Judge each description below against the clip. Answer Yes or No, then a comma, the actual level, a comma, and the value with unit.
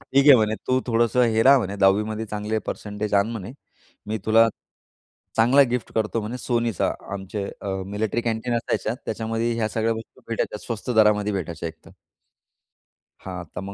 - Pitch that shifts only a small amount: Yes, narrow, 2.0 semitones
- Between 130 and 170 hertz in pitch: No, low, 110 Hz